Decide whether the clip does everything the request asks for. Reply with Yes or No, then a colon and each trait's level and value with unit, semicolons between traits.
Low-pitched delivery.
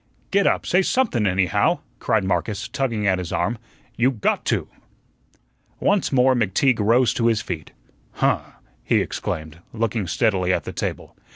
Yes: low, 110 Hz